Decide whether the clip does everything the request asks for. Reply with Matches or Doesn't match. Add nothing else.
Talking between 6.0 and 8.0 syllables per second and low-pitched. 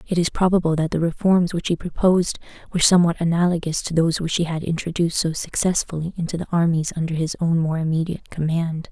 Doesn't match